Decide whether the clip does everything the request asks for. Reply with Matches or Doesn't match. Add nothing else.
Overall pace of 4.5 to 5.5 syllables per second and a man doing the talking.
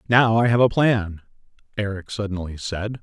Matches